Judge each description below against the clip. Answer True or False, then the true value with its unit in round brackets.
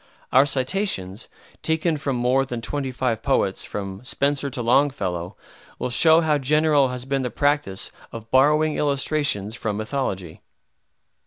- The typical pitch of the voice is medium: False (130 Hz)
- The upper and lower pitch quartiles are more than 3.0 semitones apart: True (4.4 semitones)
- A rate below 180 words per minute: True (140 wpm)